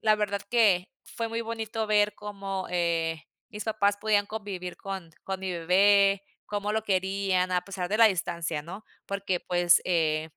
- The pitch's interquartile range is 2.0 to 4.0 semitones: Yes, average, 2.7 semitones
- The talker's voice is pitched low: No, high, 195 Hz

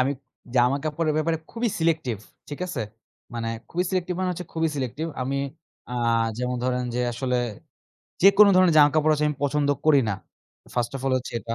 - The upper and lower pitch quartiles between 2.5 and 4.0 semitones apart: No, average, 4.7 semitones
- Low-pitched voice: No, medium, 150 Hz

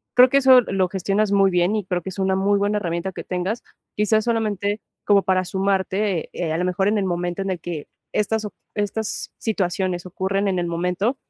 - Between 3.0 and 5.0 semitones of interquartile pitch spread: No, narrow, 2.6 semitones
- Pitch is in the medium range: No, high, 195 Hz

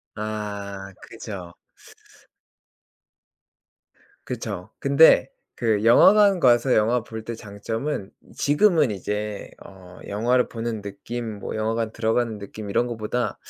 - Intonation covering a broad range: No, average, 2.9 semitones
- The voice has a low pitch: Yes, low, 110 Hz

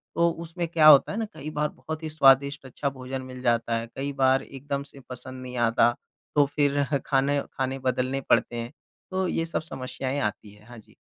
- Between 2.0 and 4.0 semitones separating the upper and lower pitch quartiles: Yes, average, 2.8 semitones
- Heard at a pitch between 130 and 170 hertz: Yes, low, 135 Hz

